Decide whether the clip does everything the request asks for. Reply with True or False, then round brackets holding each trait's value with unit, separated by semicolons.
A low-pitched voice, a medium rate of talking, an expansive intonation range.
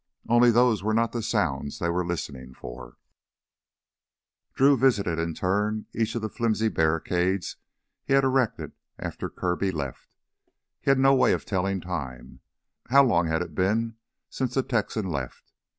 True (100 Hz; 155 wpm; 5.8 semitones)